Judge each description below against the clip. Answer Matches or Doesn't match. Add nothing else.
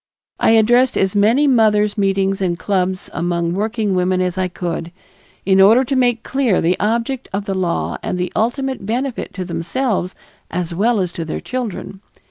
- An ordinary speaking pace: Matches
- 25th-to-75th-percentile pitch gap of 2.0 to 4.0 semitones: Doesn't match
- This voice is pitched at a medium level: Doesn't match